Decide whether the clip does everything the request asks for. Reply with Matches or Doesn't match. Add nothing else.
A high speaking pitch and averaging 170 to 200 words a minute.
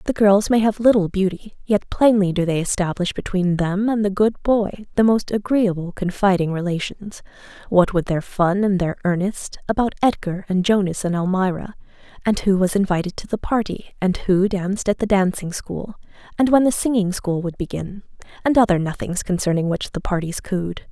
Matches